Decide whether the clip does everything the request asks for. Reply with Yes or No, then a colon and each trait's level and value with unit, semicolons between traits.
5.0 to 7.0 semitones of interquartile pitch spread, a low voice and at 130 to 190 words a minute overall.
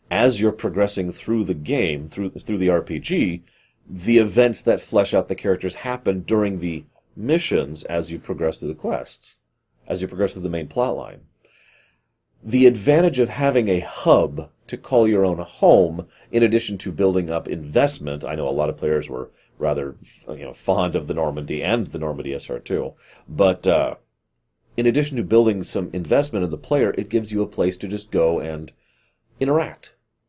Yes: average, 5.3 semitones; very low, 95 Hz; average, 180 wpm